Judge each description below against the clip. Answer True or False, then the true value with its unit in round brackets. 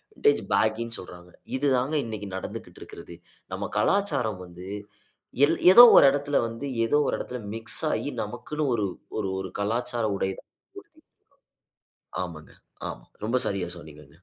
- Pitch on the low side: True (110 Hz)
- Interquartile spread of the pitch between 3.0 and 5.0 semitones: False (5.6 semitones)